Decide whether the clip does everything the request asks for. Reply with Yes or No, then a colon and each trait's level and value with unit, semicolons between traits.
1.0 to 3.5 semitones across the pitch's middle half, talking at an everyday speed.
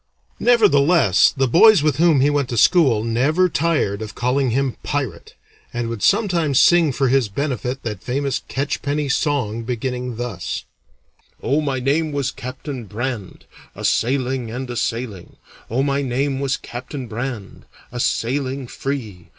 Yes: average, 3.2 semitones; average, 150 wpm